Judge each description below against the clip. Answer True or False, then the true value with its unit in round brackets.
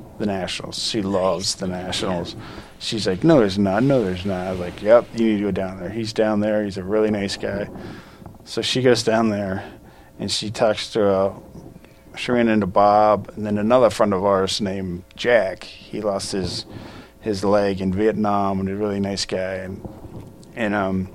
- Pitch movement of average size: False (2.1 semitones)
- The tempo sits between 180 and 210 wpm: True (195 wpm)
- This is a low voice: True (100 Hz)